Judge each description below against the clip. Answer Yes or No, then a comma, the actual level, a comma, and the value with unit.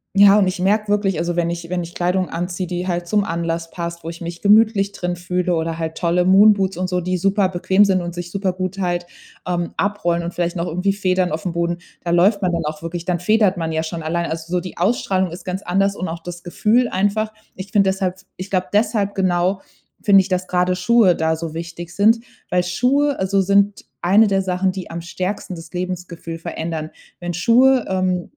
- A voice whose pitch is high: No, medium, 180 Hz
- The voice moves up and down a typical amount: No, narrow, 2.3 semitones